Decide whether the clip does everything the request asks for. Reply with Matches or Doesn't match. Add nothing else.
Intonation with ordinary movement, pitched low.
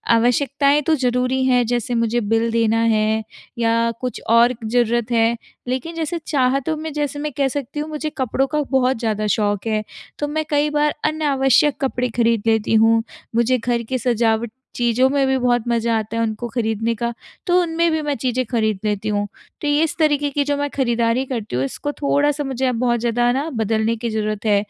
Doesn't match